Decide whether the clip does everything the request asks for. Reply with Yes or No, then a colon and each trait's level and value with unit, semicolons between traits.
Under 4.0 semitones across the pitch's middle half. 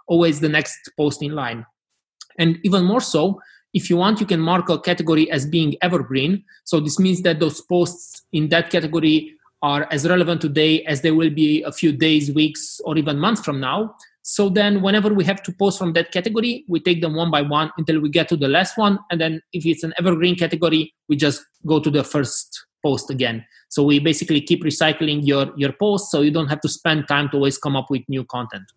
Yes: average, 3.0 semitones